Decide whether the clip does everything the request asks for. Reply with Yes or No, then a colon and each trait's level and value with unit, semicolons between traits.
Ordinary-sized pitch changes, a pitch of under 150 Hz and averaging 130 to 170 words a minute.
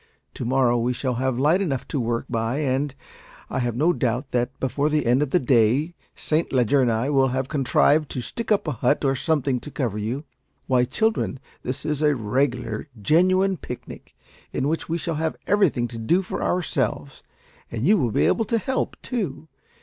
No: average, 4.3 semitones; low, 135 Hz; average, 195 wpm